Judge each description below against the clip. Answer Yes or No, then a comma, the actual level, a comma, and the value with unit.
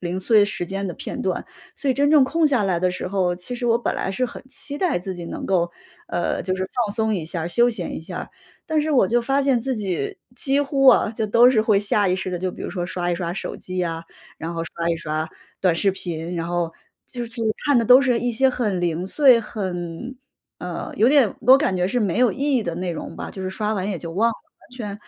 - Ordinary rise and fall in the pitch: No, wide, 5.7 semitones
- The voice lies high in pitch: Yes, high, 200 Hz